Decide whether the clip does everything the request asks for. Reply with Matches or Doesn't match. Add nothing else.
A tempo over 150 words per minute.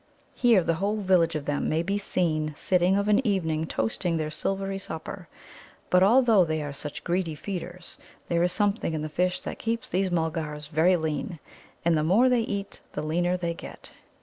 Matches